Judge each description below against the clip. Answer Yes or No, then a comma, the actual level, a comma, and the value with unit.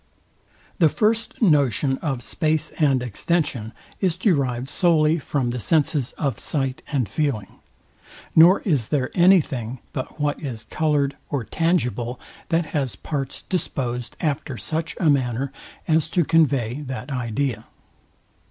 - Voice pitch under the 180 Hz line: Yes, medium, 140 Hz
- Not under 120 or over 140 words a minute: Yes, slow, 135 wpm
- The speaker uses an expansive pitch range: No, average, 4.4 semitones